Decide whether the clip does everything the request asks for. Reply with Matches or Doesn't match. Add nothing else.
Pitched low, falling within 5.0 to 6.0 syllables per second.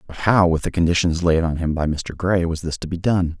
Matches